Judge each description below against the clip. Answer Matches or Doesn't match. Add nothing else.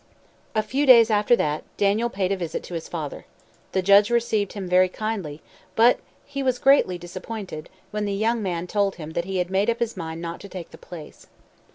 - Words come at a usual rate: Doesn't match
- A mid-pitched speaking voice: Doesn't match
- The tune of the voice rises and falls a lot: Doesn't match